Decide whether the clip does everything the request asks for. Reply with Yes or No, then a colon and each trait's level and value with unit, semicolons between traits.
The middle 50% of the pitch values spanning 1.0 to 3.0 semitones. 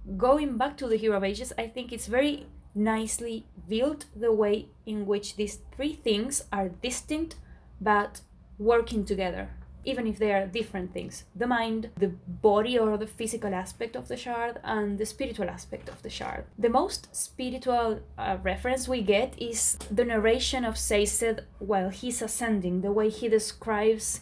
Yes: average, 2.7 semitones